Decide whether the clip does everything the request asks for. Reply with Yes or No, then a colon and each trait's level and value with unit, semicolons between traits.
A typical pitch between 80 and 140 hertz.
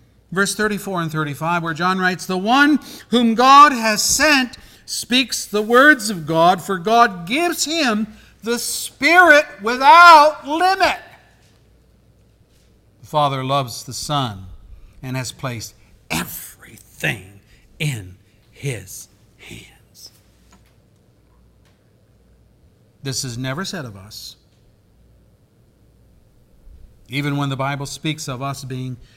Yes: low, 135 Hz